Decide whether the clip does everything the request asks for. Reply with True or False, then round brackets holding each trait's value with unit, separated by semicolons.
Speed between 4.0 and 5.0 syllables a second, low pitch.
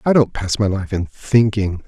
True (4.6 syllables/s; 105 Hz)